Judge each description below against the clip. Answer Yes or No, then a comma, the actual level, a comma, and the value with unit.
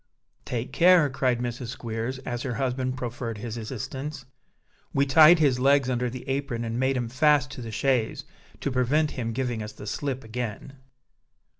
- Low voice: Yes, low, 130 Hz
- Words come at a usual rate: Yes, average, 170 wpm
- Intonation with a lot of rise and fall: No, narrow, 2.6 semitones